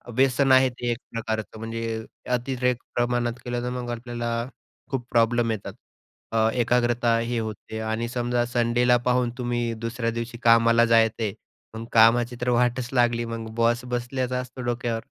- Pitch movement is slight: Yes, narrow, 1.1 semitones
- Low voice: Yes, low, 120 Hz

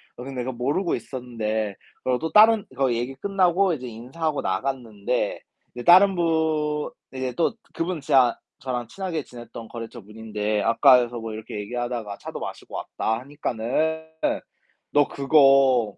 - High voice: No, low, 130 Hz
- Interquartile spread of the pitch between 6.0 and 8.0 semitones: No, average, 5.3 semitones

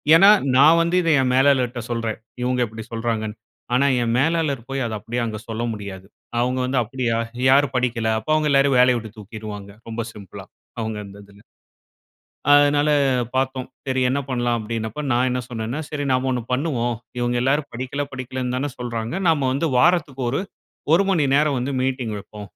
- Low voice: Yes, low, 125 Hz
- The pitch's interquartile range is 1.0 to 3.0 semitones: No, average, 3.5 semitones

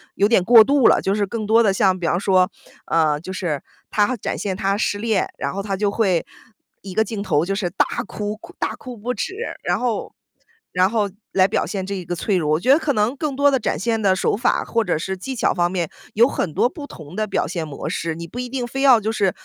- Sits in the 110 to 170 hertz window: No, high, 200 Hz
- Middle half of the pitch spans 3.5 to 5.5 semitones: Yes, average, 4.1 semitones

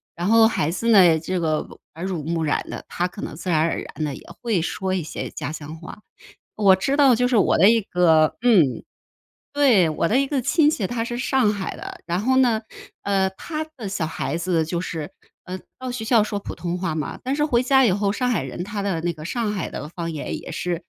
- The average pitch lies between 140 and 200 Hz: Yes, high, 190 Hz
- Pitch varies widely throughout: Yes, wide, 6.0 semitones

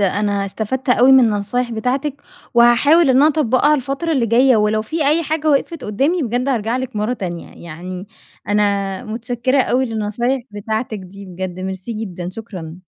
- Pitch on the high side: Yes, high, 230 Hz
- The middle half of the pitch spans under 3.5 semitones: No, average, 4.5 semitones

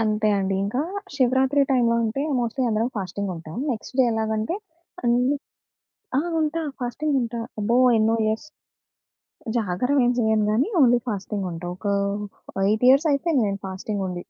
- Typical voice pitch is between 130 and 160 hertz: No, high, 225 Hz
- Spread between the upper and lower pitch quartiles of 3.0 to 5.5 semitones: Yes, average, 3.6 semitones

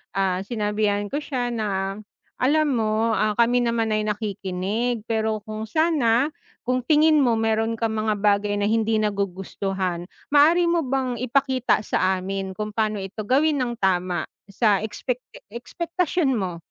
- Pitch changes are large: No, average, 3.8 semitones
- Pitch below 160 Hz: No, high, 220 Hz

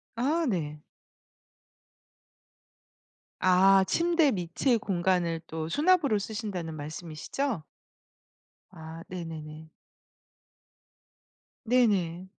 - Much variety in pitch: Yes, wide, 6.3 semitones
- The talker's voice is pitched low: No, medium, 185 Hz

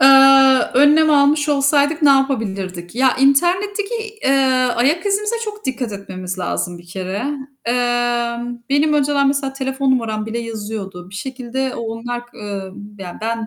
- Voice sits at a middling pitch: No, very high, 255 Hz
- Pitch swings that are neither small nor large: Yes, average, 4.3 semitones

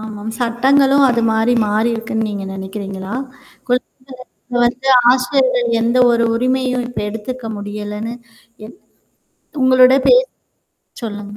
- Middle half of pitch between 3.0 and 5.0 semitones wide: Yes, average, 3.3 semitones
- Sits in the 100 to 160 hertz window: No, high, 235 Hz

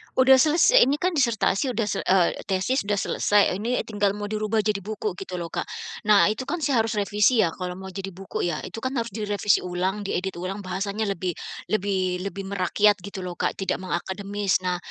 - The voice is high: Yes, high, 200 Hz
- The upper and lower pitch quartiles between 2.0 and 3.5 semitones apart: Yes, narrow, 2.5 semitones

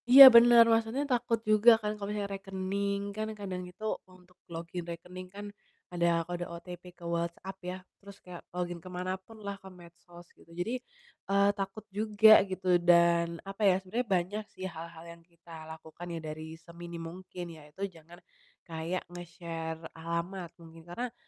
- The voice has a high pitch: No, medium, 180 Hz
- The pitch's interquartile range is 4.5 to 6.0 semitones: No, average, 2.9 semitones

